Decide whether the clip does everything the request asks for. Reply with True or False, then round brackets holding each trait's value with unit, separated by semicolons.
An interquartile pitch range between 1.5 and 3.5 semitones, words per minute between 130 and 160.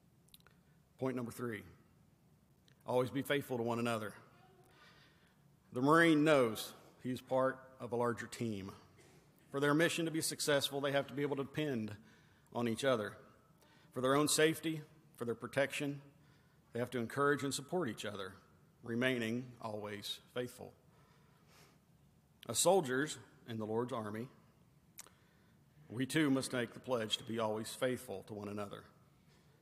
False (3.9 semitones; 145 wpm)